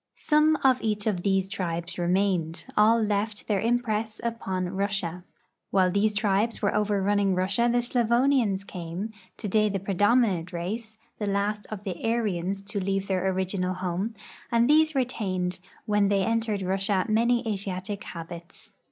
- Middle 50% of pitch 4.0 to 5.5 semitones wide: No, average, 3.1 semitones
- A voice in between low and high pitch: No, high, 200 Hz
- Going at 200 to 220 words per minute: No, average, 150 wpm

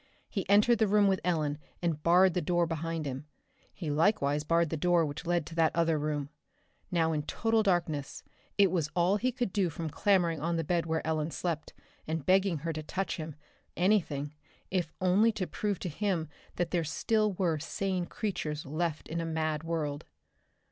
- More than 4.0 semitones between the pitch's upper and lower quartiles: No, average, 3.3 semitones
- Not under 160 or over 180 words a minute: No, average, 190 wpm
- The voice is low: No, medium, 170 Hz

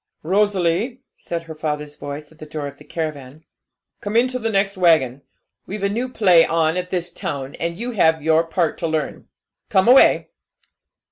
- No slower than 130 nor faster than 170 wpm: No, average, 180 wpm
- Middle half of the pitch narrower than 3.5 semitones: No, average, 4.4 semitones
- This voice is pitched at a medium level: Yes, medium, 165 Hz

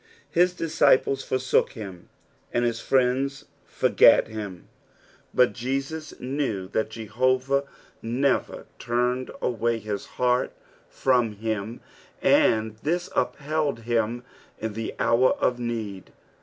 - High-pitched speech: No, low, 125 Hz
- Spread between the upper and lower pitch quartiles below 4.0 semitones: Yes, average, 3.3 semitones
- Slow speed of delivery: Yes, slow, 110 wpm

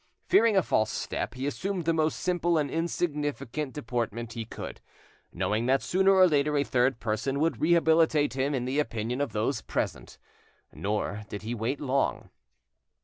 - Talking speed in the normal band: Yes, average, 165 wpm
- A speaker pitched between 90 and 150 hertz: Yes, medium, 140 Hz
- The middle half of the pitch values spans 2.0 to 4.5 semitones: No, average, 5.3 semitones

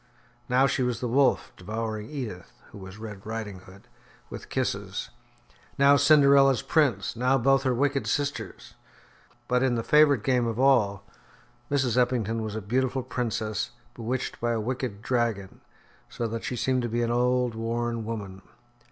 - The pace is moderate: Yes, average, 160 wpm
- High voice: No, low, 120 Hz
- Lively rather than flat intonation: No, average, 3.0 semitones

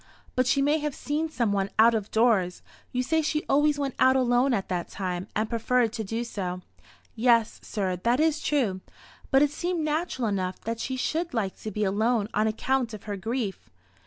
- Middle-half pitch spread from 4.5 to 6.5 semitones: Yes, average, 4.9 semitones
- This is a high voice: Yes, high, 235 Hz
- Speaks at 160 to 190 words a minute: No, average, 200 wpm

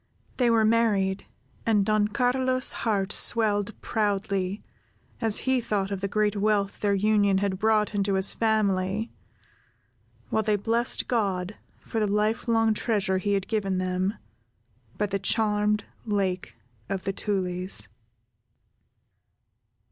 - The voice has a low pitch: No, high, 205 Hz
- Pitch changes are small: Yes, narrow, 2.0 semitones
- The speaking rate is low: Yes, slow, 125 wpm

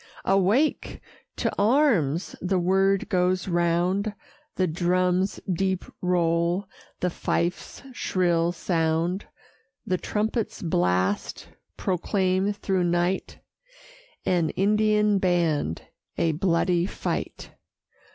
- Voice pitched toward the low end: No, medium, 180 Hz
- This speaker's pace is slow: Yes, slow, 90 wpm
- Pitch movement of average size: No, narrow, 2.2 semitones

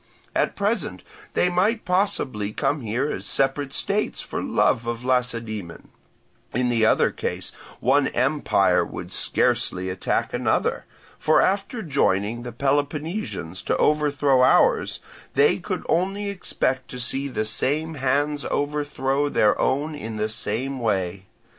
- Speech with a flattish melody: No, average, 4.6 semitones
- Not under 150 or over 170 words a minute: No, slow, 135 wpm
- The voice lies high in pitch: No, low, 135 Hz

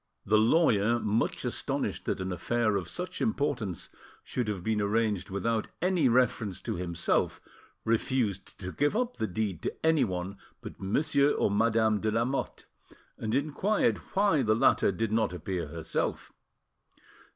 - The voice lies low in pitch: Yes, low, 110 Hz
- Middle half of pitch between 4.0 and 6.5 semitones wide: Yes, average, 5.1 semitones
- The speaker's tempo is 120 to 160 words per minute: Yes, average, 145 wpm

